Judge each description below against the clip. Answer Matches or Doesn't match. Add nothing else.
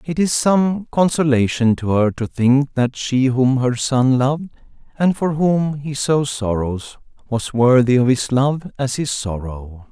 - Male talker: Matches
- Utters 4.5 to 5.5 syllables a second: Doesn't match